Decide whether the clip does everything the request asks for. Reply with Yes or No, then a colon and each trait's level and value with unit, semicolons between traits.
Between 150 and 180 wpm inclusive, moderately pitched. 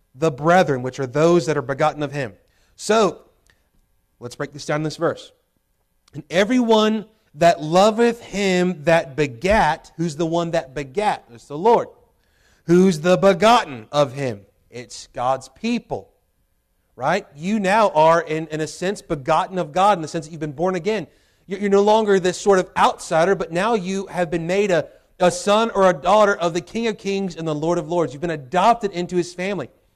No: average, 190 wpm; medium, 175 Hz